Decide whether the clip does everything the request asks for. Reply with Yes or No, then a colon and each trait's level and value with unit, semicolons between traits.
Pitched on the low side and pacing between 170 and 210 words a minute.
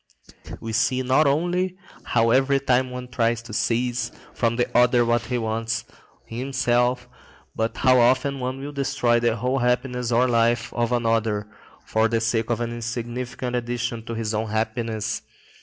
No: low, 120 Hz; average, 155 wpm